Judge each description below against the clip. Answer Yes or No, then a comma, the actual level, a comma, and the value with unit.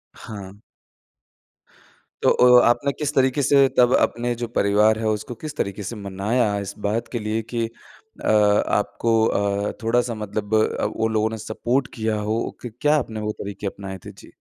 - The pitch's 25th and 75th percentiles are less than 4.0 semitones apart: Yes, average, 2.9 semitones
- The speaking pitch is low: Yes, low, 110 Hz